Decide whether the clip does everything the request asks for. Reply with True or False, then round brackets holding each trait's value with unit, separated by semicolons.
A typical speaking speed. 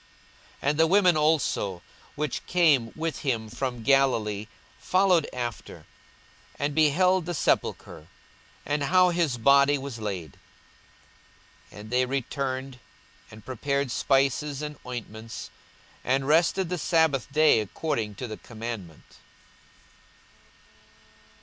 False (115 wpm)